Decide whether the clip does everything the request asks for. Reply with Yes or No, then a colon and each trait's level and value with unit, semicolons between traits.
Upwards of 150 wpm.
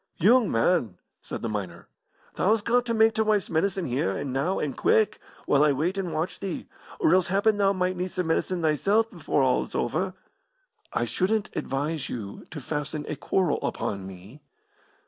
Yes: average, 185 wpm